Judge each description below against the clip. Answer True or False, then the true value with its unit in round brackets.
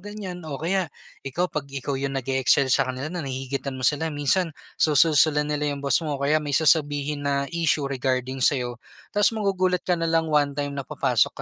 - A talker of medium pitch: True (145 Hz)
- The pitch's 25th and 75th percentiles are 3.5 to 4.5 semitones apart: False (3.0 semitones)